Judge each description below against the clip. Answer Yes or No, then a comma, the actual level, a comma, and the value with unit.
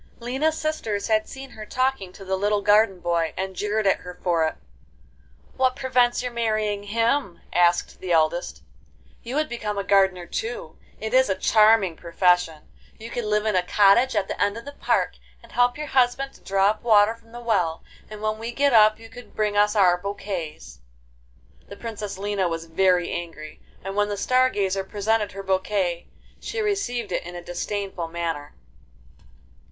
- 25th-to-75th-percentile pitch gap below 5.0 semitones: Yes, average, 4.0 semitones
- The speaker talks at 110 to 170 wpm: No, average, 185 wpm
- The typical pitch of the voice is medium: No, high, 205 Hz